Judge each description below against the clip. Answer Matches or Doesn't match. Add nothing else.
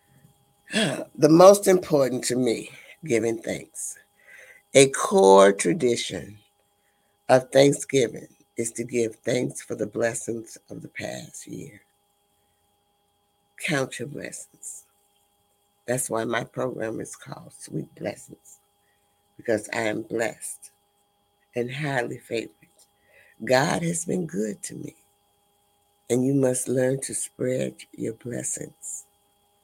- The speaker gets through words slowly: Matches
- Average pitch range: Matches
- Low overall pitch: Matches